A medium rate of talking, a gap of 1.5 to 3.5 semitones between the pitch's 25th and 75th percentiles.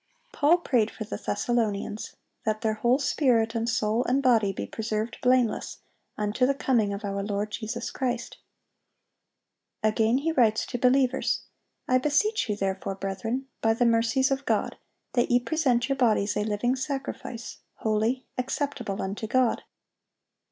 Yes: average, 150 wpm; average, 3.1 semitones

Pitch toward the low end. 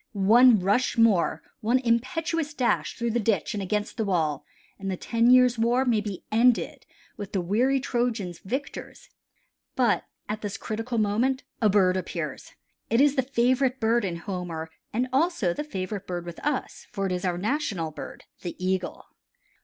No: high, 220 Hz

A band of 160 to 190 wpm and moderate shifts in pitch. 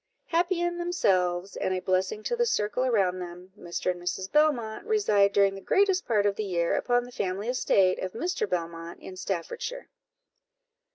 No: average, 175 wpm; wide, 6.0 semitones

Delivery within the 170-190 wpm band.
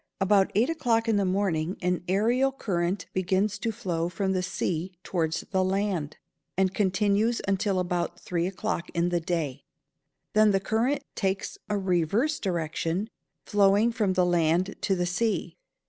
No: average, 155 wpm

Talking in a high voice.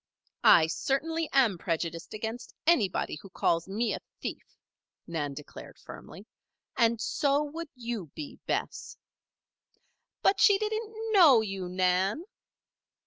Yes: high, 225 Hz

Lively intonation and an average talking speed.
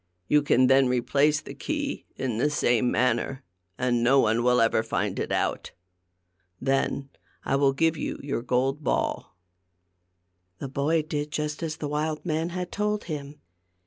No: average, 3.3 semitones; average, 160 wpm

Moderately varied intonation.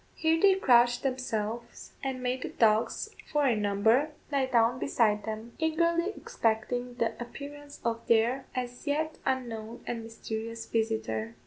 Yes: average, 3.4 semitones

